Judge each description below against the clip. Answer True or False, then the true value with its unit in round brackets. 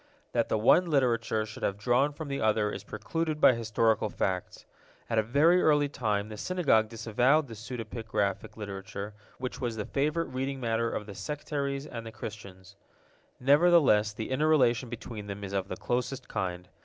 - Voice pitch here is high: False (115 Hz)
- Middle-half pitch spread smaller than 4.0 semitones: False (4.6 semitones)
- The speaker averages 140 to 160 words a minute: False (175 wpm)